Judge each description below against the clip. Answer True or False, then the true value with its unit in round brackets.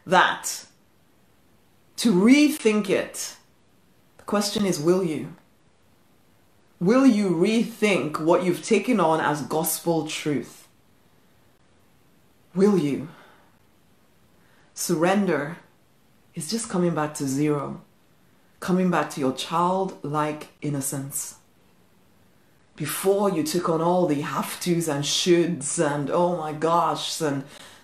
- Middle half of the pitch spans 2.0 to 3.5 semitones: False (4.0 semitones)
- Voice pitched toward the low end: False (170 Hz)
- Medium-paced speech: False (105 wpm)